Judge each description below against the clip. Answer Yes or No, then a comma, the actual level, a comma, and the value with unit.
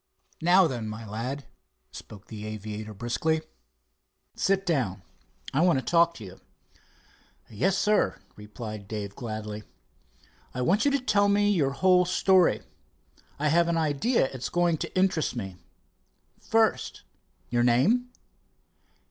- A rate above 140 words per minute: No, slow, 135 wpm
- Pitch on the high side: No, medium, 140 Hz